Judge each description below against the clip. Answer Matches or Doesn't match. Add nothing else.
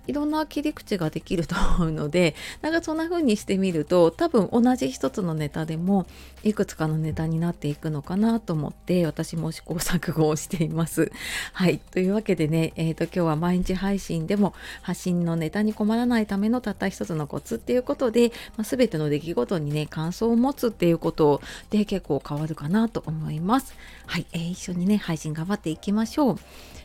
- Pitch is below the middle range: Doesn't match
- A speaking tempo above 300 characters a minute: Matches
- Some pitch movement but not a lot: Matches